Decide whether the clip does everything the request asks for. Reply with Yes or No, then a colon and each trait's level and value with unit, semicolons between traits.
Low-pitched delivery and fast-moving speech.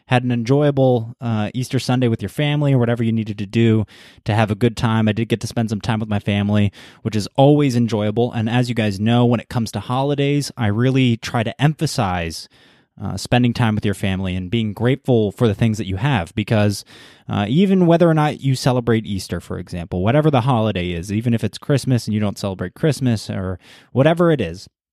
Yes: low, 115 Hz; fast, 220 wpm